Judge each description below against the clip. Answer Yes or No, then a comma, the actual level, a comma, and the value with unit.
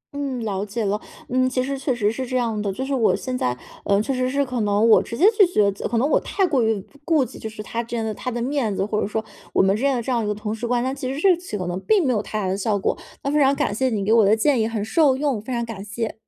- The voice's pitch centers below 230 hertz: No, high, 235 Hz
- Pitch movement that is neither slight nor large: Yes, average, 4.0 semitones